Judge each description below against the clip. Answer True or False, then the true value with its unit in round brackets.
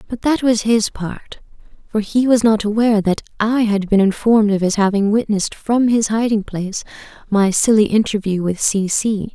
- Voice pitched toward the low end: False (215 Hz)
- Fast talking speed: False (185 wpm)